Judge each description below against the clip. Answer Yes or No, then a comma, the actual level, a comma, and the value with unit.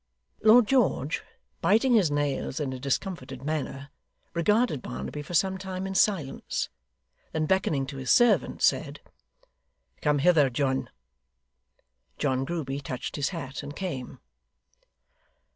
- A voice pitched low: No, medium, 150 Hz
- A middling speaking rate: No, slow, 125 wpm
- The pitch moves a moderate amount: No, wide, 5.9 semitones